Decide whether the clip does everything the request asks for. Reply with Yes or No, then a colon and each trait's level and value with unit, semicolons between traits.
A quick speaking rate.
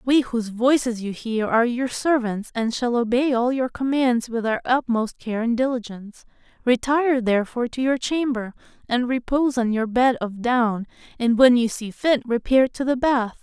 No: average, 185 wpm